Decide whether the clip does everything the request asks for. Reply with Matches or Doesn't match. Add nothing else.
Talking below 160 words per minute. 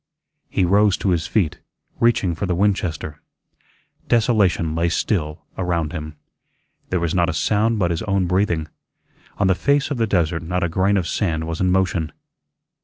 Doesn't match